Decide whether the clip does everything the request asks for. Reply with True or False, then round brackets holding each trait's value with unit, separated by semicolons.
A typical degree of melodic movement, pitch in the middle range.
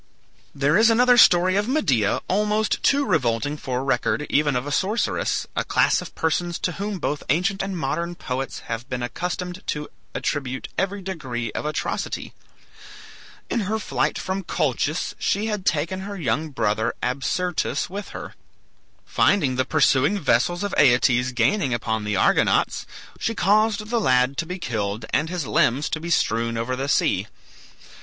False (7.2 semitones; 155 Hz)